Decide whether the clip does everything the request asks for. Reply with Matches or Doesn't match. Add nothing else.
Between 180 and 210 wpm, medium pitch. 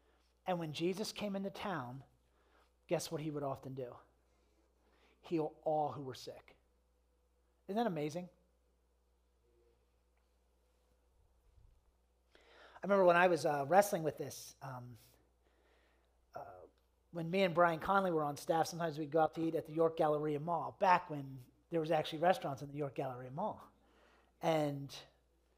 Doesn't match